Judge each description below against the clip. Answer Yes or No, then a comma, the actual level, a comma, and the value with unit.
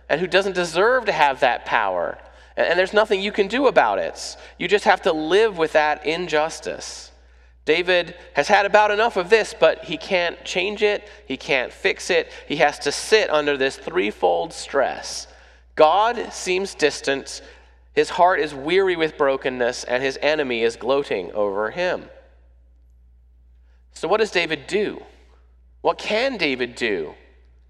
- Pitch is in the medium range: Yes, medium, 155 Hz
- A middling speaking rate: Yes, average, 160 wpm